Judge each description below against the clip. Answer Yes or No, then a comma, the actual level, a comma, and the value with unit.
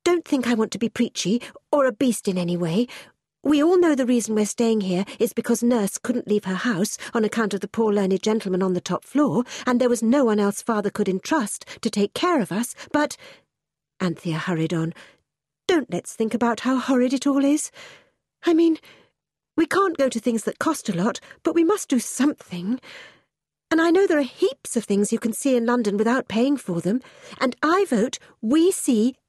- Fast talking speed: Yes, fast, 215 wpm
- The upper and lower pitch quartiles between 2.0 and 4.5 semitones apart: No, average, 5.3 semitones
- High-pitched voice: Yes, high, 240 Hz